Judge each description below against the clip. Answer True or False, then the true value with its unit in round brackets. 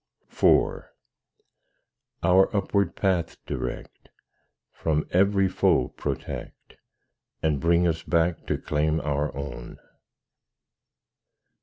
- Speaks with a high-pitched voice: False (85 Hz)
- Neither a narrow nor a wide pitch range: True (3.5 semitones)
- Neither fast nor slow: False (90 wpm)